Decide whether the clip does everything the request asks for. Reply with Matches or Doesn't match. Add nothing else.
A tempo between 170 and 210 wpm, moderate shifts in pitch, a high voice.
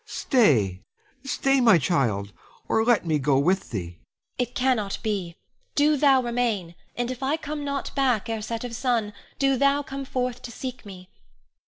Doesn't match